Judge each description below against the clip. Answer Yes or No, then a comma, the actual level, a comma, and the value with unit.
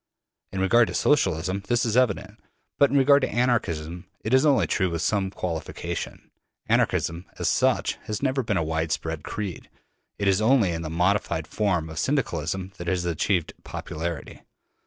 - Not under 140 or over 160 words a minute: No, average, 170 wpm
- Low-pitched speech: Yes, very low, 95 Hz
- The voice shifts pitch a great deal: Yes, wide, 5.7 semitones